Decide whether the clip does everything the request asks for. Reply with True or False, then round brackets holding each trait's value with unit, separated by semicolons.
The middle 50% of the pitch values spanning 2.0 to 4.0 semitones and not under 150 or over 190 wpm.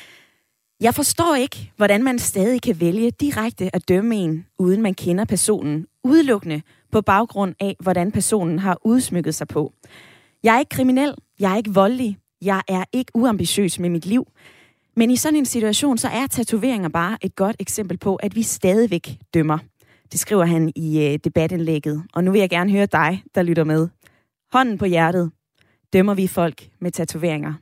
False (5.3 semitones; 175 wpm)